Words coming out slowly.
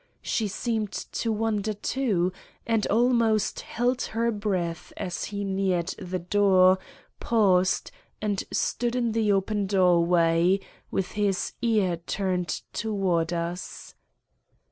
Yes: slow, 115 wpm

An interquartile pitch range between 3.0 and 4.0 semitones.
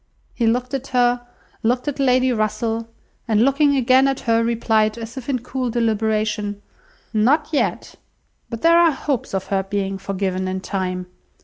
Yes: average, 3.4 semitones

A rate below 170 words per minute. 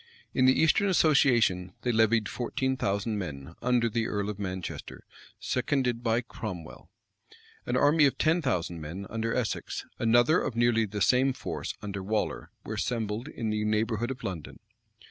Yes: average, 160 wpm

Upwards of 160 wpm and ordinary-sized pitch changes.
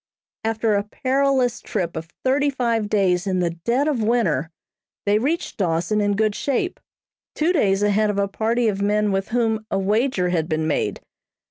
Yes: average, 175 wpm; average, 3.8 semitones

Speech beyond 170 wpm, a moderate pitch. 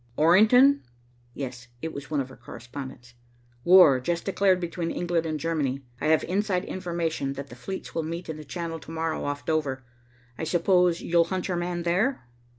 Yes: average, 180 wpm; medium, 165 Hz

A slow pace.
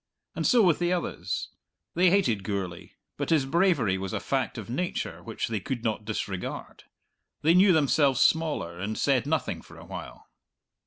No: average, 170 wpm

